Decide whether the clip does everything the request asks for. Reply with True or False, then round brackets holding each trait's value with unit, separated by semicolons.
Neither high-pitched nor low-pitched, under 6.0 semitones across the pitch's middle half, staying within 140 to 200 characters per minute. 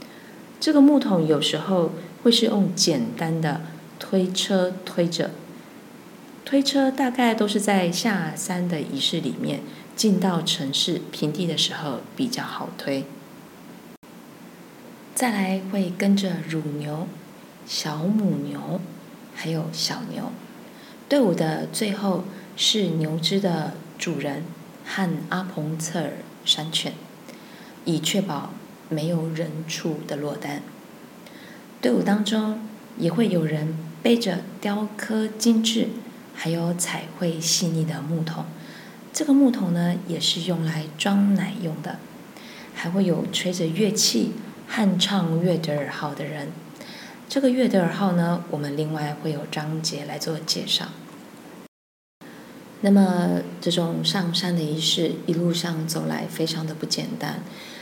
True (180 Hz; 5.2 semitones; 185 characters per minute)